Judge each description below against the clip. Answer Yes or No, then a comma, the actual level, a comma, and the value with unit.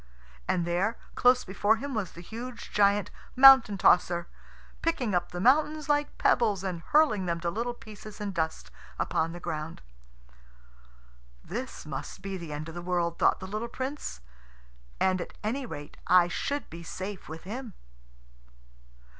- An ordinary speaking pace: Yes, average, 155 wpm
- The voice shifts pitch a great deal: Yes, wide, 5.8 semitones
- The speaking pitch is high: Yes, high, 195 Hz